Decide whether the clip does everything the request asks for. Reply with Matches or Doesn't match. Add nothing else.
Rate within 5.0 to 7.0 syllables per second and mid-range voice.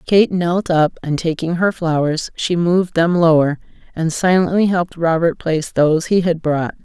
Doesn't match